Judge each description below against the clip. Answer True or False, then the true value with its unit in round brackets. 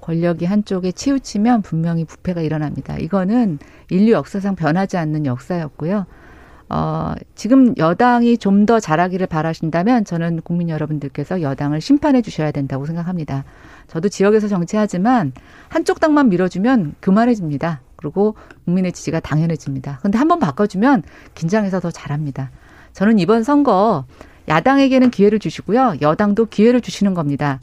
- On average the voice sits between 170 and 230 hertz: True (185 Hz)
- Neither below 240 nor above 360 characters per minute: False (370 characters per minute)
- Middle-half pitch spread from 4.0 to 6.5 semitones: True (6.1 semitones)